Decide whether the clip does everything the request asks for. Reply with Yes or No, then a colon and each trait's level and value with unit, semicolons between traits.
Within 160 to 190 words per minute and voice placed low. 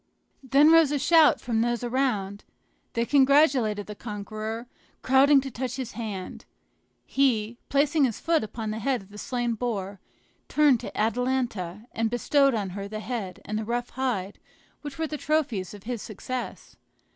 No: average, 165 wpm; high, 240 Hz